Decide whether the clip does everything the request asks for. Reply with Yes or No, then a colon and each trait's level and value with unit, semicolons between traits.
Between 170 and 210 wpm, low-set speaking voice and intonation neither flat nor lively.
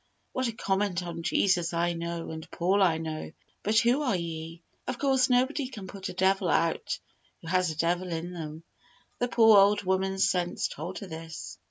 No: average, 190 wpm; medium, 185 Hz; average, 3.6 semitones